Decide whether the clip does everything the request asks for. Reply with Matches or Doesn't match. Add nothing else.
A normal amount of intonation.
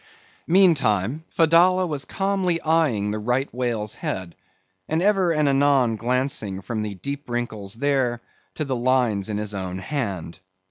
Doesn't match